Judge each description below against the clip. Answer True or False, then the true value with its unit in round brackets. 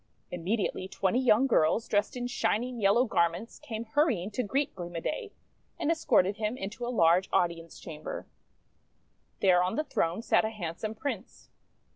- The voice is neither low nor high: False (220 Hz)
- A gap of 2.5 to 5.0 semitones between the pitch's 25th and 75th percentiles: False (5.5 semitones)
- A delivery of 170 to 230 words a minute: False (160 wpm)